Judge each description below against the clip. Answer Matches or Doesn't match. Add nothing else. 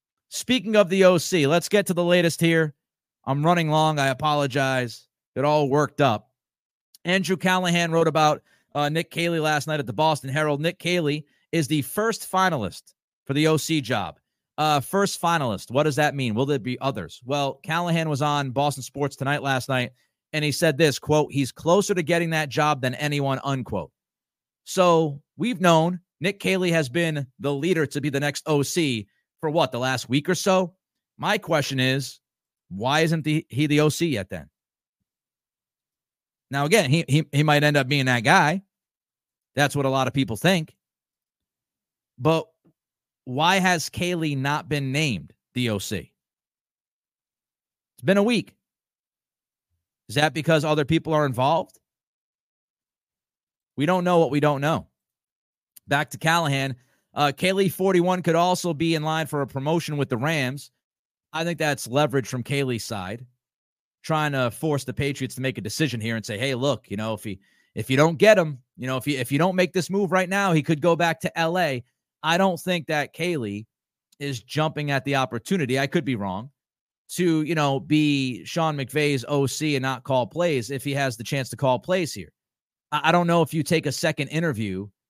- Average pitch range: Matches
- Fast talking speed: Doesn't match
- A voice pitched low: Doesn't match